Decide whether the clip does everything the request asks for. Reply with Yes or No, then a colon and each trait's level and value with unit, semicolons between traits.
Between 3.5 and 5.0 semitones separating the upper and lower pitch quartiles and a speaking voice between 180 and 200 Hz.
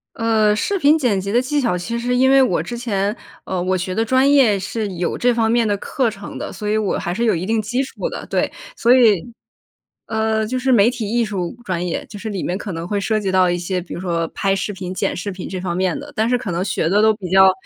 No: average, 4.1 semitones; high, 210 Hz